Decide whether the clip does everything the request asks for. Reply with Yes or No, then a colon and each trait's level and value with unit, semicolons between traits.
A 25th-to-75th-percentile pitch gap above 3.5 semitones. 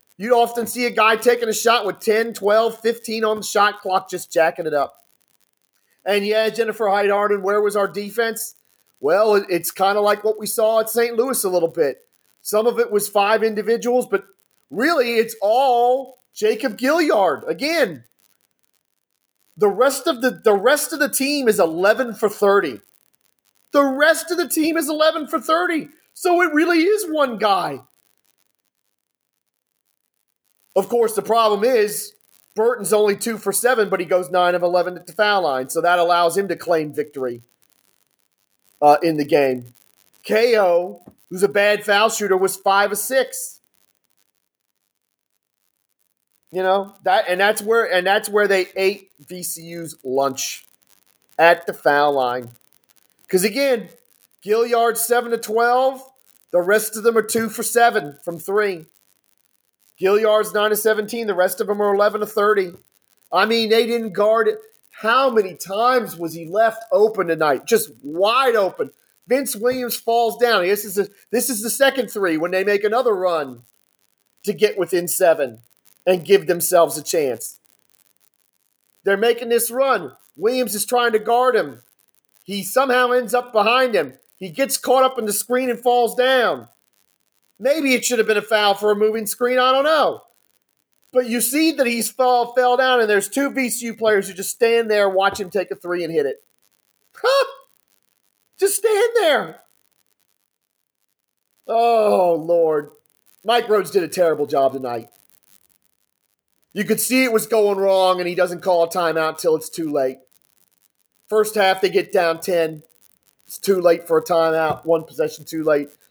Yes: average, 5.1 semitones